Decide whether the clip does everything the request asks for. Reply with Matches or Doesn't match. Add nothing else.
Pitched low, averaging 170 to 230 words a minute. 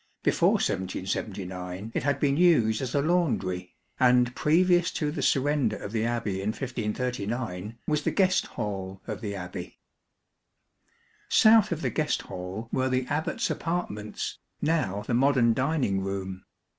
Doesn't match